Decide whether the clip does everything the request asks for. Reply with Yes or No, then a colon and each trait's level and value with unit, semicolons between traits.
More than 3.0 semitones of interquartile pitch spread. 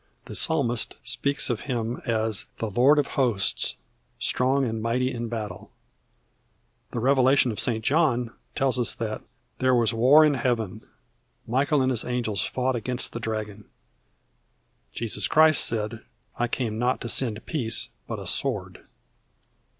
No: average, 2.7 semitones